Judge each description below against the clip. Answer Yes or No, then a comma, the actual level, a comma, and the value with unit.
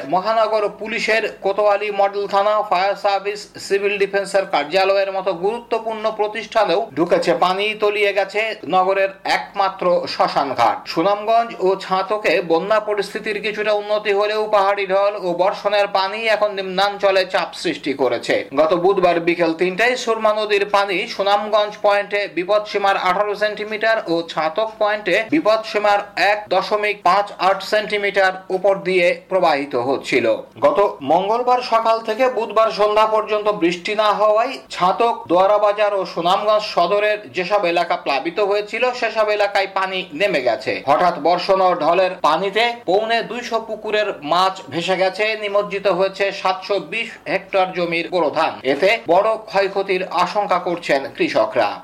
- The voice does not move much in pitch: Yes, narrow, 2.2 semitones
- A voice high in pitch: Yes, high, 205 Hz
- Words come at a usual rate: No, fast, 130 wpm